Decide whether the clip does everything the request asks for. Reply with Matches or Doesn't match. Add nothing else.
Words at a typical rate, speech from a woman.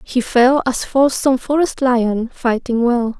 Matches